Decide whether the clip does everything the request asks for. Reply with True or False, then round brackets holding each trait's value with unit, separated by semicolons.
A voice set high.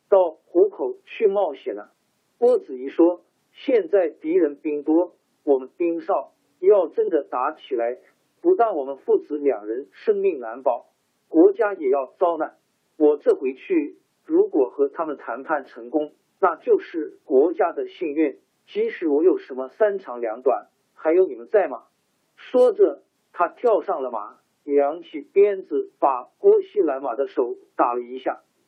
True (375 Hz)